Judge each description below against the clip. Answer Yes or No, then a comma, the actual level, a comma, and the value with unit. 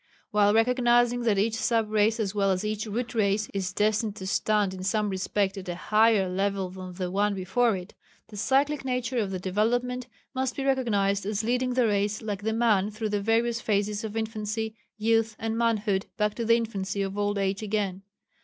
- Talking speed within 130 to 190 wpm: No, average, 200 wpm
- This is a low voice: No, high, 210 Hz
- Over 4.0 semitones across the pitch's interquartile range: No, narrow, 2.4 semitones